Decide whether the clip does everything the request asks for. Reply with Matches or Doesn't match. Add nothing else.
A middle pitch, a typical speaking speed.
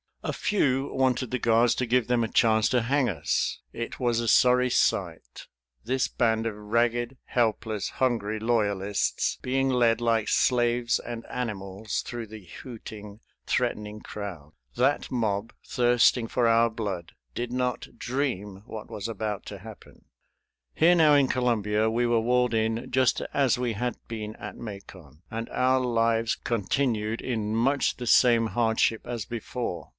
Doesn't match